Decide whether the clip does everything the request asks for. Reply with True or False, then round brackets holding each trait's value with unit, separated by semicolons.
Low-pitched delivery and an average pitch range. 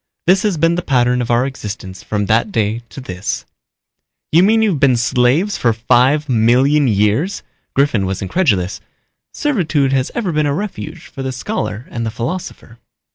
False (130 Hz; 6.5 semitones)